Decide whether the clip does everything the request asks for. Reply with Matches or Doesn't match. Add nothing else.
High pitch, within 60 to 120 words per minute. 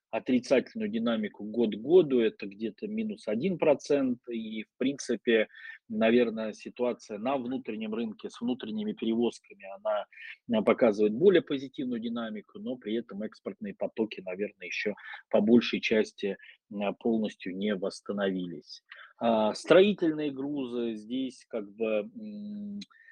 Doesn't match